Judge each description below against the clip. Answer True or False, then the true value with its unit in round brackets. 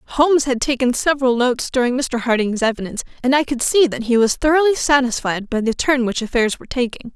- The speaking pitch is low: False (255 Hz)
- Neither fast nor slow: False (210 wpm)